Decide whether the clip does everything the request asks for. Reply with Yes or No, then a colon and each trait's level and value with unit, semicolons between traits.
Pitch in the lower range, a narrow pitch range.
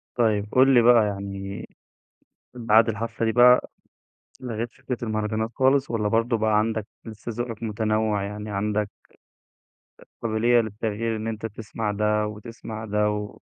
Yes: low, 110 Hz; narrow, 1.5 semitones